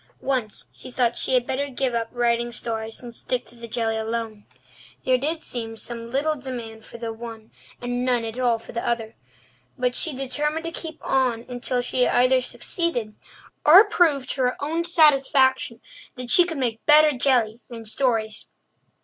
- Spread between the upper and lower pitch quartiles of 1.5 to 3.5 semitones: Yes, average, 2.8 semitones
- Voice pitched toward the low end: No, high, 245 Hz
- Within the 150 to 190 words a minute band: Yes, average, 175 wpm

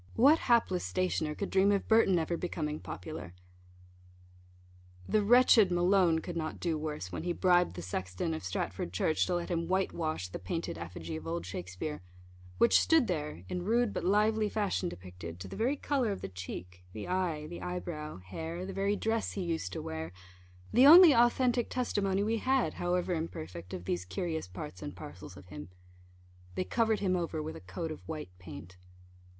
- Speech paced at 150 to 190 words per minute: Yes, average, 185 wpm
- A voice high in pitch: No, medium, 170 Hz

